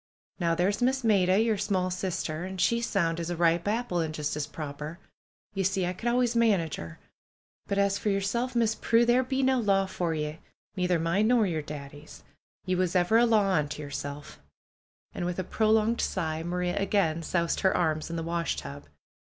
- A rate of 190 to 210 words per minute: Yes, average, 195 wpm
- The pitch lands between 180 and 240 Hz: Yes, medium, 185 Hz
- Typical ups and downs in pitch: Yes, average, 4.6 semitones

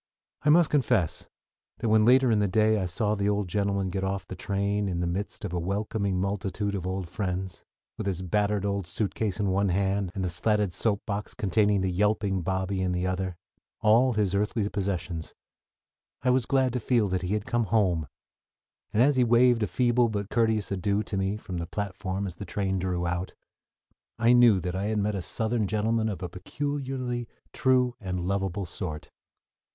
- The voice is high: No, low, 100 Hz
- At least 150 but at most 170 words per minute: No, average, 200 wpm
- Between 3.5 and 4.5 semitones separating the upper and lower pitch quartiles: No, average, 2.8 semitones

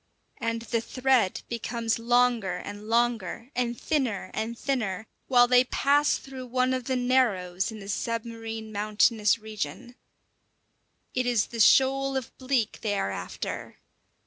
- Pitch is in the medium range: No, high, 235 Hz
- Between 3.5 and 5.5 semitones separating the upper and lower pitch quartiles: No, average, 2.8 semitones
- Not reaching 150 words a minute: Yes, average, 140 wpm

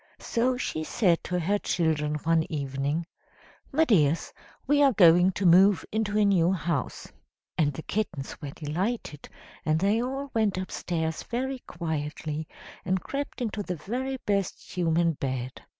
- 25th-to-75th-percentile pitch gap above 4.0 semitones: Yes, wide, 5.5 semitones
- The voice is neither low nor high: Yes, medium, 180 Hz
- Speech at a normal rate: Yes, average, 150 wpm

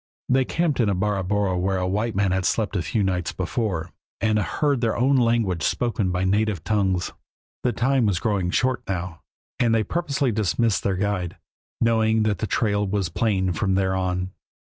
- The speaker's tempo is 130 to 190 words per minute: Yes, average, 180 wpm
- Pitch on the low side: Yes, low, 105 Hz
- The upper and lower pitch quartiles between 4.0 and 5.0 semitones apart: No, average, 3.6 semitones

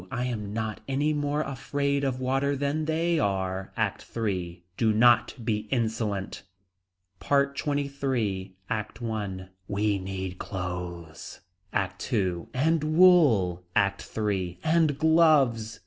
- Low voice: Yes, low, 115 Hz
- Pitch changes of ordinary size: No, wide, 6.6 semitones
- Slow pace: Yes, slow, 120 wpm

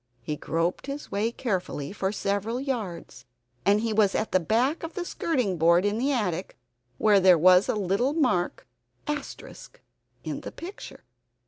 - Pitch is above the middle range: Yes, high, 205 Hz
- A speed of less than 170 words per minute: Yes, average, 155 wpm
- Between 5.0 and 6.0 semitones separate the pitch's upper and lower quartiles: Yes, wide, 5.5 semitones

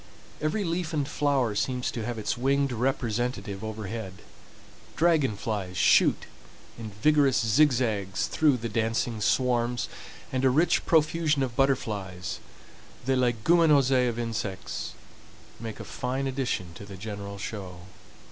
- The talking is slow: Yes, slow, 120 wpm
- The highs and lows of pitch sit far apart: No, average, 4.4 semitones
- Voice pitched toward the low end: Yes, low, 120 Hz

